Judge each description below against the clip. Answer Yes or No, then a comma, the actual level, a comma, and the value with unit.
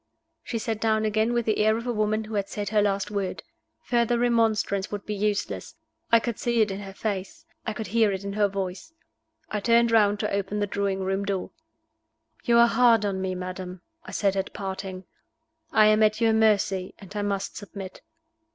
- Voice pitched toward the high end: Yes, high, 210 Hz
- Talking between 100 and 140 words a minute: No, fast, 205 wpm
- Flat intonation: Yes, narrow, 2.1 semitones